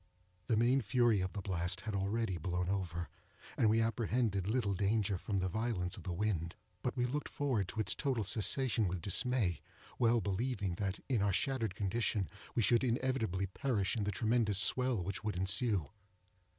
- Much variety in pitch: No, average, 3.9 semitones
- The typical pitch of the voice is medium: No, low, 105 Hz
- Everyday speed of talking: Yes, average, 175 wpm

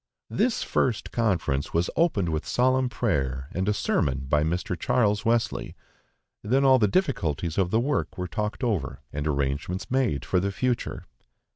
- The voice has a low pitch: Yes, low, 100 Hz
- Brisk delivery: No, average, 160 wpm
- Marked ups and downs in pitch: Yes, wide, 7.8 semitones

